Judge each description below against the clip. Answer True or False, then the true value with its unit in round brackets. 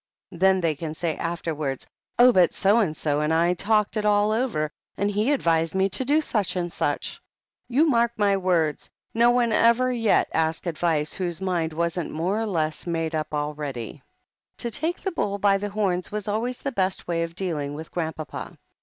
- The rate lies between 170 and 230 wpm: True (190 wpm)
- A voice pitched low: False (185 Hz)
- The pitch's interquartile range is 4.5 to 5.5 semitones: True (4.9 semitones)